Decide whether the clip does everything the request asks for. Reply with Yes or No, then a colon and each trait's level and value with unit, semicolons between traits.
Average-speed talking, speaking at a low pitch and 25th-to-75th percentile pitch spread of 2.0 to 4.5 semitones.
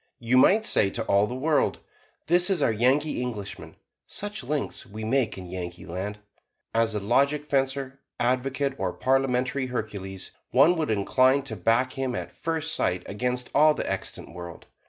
No: average, 160 wpm; low, 125 Hz; average, 5.1 semitones